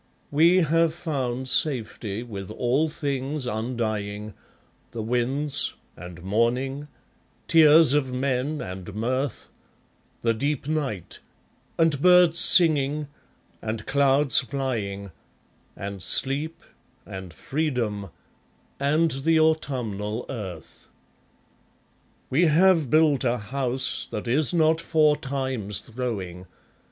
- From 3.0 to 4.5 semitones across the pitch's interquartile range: No, wide, 5.6 semitones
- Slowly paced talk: Yes, slow, 100 wpm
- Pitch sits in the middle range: No, low, 130 Hz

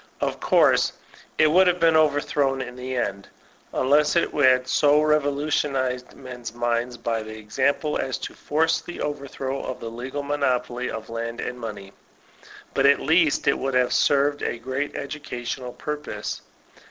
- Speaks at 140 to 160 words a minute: Yes, average, 155 wpm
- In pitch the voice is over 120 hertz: Yes, low, 135 Hz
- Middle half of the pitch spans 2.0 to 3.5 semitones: Yes, average, 3.1 semitones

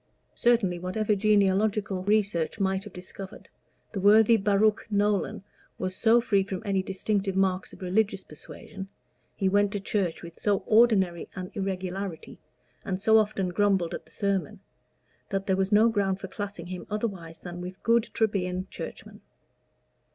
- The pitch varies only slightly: Yes, narrow, 2.0 semitones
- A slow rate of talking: No, average, 150 wpm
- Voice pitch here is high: Yes, high, 195 Hz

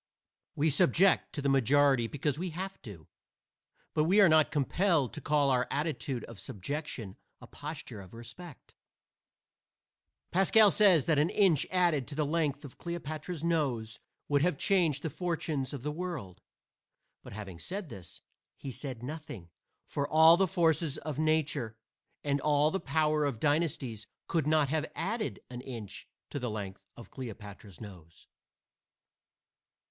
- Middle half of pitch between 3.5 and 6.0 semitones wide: Yes, average, 4.9 semitones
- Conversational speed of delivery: Yes, average, 150 wpm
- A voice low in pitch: No, medium, 145 Hz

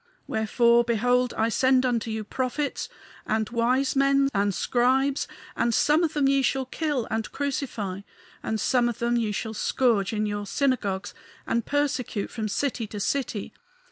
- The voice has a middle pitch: No, high, 240 Hz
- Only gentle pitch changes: No, average, 3.6 semitones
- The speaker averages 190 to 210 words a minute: No, average, 160 wpm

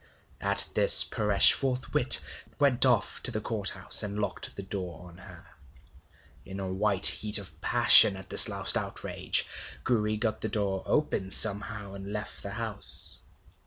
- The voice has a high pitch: No, low, 105 Hz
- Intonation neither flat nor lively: No, narrow, 1.9 semitones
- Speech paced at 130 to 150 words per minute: No, average, 160 wpm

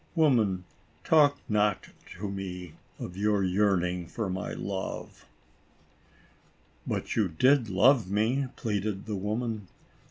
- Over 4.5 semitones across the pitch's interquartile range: No, average, 3.3 semitones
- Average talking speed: No, slow, 115 wpm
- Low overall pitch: Yes, low, 105 Hz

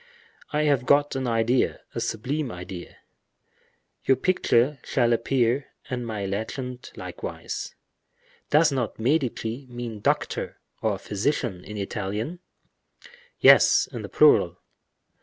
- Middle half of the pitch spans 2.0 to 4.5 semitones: Yes, average, 3.7 semitones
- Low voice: Yes, low, 120 Hz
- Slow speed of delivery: Yes, slow, 110 wpm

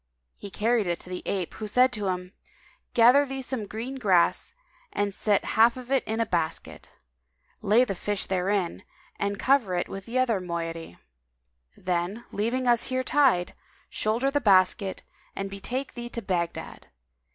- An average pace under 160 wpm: No, average, 165 wpm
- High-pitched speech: Yes, high, 210 Hz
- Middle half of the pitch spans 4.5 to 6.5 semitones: Yes, average, 4.8 semitones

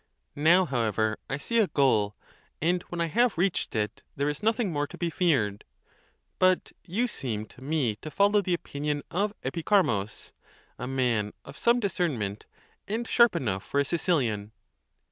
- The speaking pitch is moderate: Yes, medium, 150 Hz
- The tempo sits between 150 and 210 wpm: Yes, average, 165 wpm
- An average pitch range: No, wide, 8.3 semitones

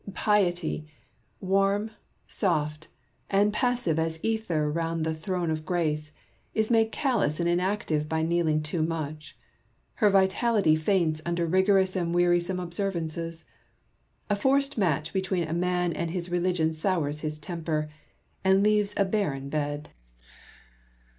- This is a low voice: No, medium, 175 Hz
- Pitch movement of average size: Yes, average, 3.8 semitones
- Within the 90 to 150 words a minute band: Yes, average, 140 wpm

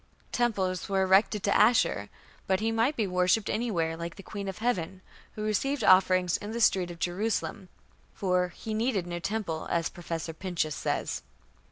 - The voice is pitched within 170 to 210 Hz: Yes, high, 190 Hz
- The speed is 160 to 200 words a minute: Yes, average, 170 wpm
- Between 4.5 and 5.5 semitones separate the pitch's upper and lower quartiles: No, average, 3.6 semitones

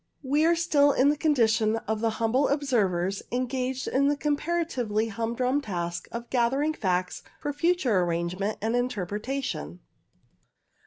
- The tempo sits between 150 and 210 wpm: No, average, 140 wpm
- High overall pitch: Yes, high, 245 Hz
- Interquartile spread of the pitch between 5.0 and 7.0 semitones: Yes, average, 5.3 semitones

